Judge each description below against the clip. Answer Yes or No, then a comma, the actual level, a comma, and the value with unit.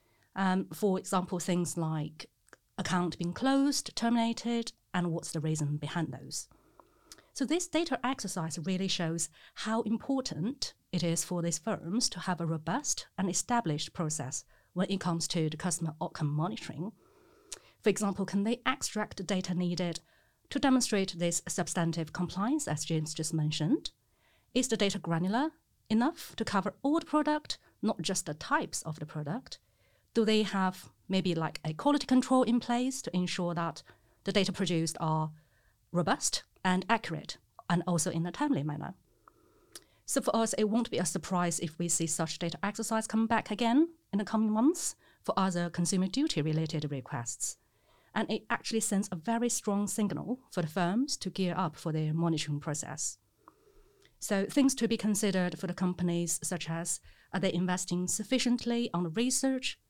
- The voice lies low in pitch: No, medium, 185 Hz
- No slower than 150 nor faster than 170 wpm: Yes, average, 165 wpm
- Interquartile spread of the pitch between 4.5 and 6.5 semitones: Yes, wide, 5.5 semitones